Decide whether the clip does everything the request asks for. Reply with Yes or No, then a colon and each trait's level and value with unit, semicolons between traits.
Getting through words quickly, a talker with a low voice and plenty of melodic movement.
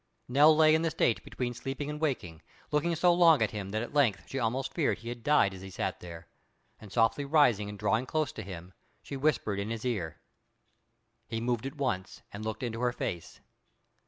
Yes: fast, 210 wpm; low, 120 Hz; wide, 5.9 semitones